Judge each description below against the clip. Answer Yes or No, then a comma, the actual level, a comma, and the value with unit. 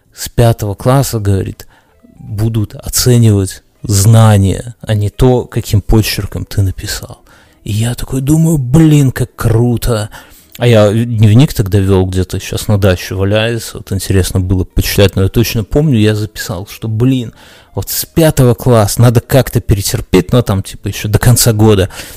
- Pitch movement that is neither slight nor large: Yes, average, 3.6 semitones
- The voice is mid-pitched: No, low, 110 Hz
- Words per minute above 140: Yes, average, 155 wpm